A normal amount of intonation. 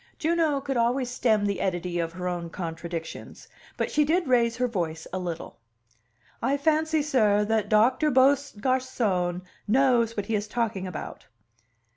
No: wide, 6.5 semitones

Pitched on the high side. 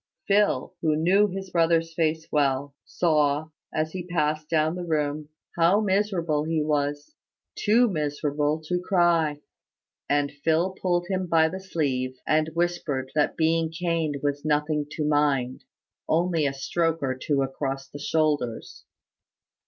No: medium, 155 Hz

